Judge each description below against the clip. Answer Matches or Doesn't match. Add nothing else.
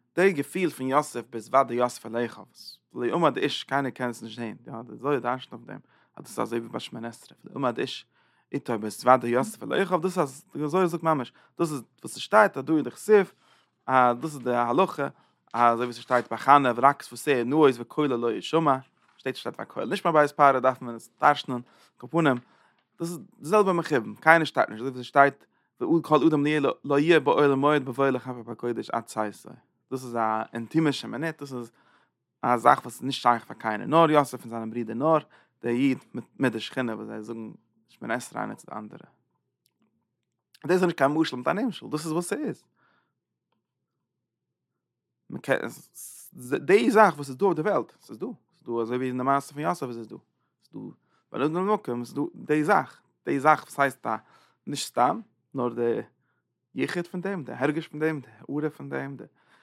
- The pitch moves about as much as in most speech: Matches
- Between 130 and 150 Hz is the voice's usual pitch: Matches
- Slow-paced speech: Doesn't match